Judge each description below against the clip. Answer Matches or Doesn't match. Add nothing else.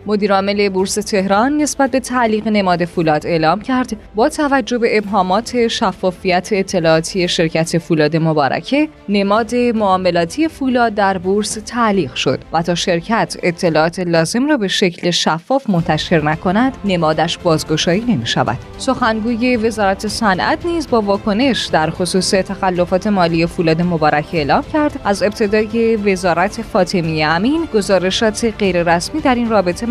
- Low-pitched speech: Doesn't match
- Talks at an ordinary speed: Matches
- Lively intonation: Doesn't match